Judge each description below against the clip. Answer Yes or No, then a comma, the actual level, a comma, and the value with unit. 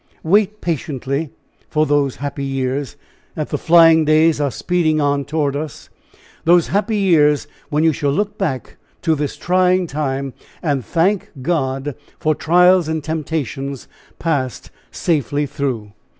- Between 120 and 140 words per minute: Yes, slow, 135 wpm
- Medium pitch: Yes, medium, 155 Hz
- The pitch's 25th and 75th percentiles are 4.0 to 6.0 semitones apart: No, average, 3.4 semitones